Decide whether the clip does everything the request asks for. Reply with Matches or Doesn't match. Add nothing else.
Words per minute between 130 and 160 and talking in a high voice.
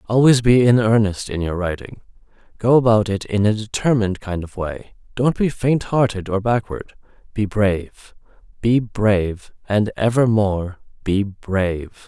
Doesn't match